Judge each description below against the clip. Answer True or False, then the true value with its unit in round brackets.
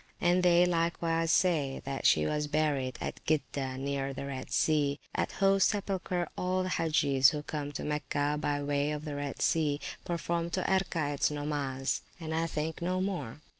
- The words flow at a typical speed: True (170 wpm)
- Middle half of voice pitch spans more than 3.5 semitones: False (3.2 semitones)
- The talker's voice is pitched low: False (150 Hz)